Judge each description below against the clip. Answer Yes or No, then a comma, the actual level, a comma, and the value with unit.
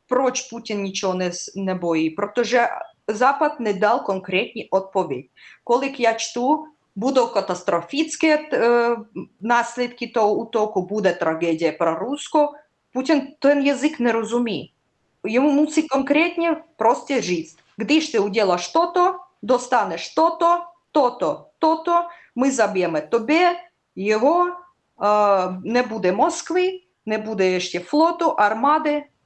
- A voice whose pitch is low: No, high, 240 Hz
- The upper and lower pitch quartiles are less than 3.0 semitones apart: No, wide, 7.3 semitones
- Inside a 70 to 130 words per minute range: Yes, slow, 115 wpm